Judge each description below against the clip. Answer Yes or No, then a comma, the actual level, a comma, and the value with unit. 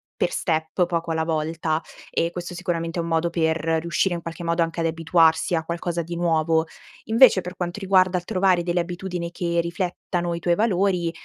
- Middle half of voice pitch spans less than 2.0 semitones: Yes, narrow, 1.4 semitones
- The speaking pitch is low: No, medium, 170 Hz